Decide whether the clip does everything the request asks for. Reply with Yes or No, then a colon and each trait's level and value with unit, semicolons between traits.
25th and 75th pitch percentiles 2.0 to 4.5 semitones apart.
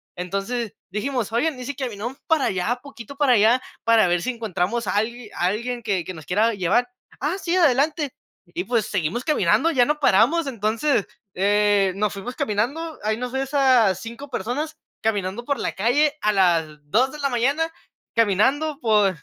No: average, 5.2 semitones